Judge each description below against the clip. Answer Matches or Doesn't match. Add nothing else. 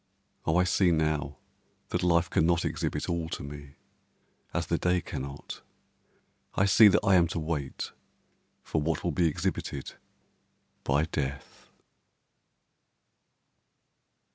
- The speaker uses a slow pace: Matches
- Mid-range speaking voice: Doesn't match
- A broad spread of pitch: Doesn't match